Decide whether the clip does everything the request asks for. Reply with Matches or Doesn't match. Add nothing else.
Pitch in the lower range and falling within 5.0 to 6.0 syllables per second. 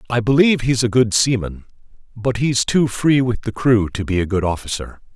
Matches